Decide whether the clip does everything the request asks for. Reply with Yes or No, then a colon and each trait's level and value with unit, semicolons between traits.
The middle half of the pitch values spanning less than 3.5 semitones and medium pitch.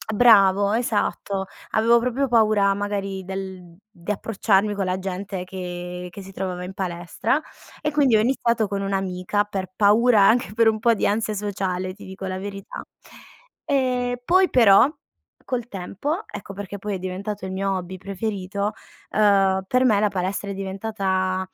No: average, 2.7 semitones; high, 200 Hz